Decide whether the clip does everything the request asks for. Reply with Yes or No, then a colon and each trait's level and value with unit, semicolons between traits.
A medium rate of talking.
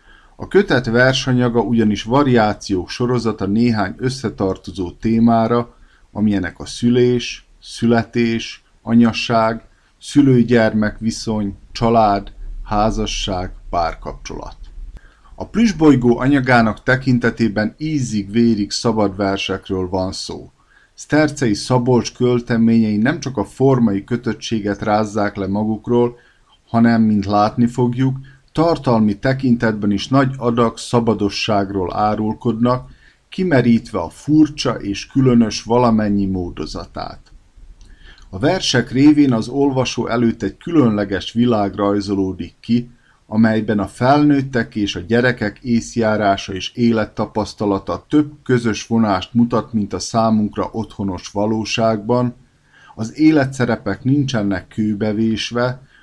No: slow, 95 wpm